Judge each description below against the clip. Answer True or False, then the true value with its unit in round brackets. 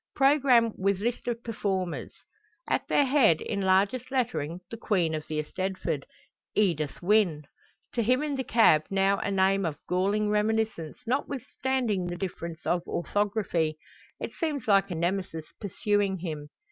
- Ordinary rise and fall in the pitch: True (4.7 semitones)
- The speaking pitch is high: True (195 Hz)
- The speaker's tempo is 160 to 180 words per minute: False (145 wpm)